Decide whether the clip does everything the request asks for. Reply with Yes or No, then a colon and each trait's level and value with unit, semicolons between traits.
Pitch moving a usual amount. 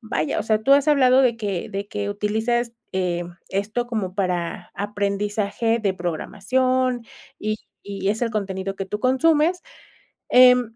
Yes: average, 3.8 semitones